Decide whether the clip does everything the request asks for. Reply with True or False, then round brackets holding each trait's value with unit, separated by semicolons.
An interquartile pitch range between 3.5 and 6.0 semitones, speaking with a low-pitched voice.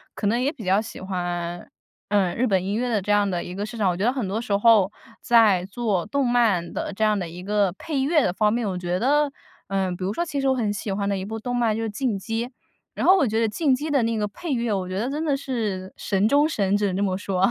False (4.0 semitones; 210 Hz)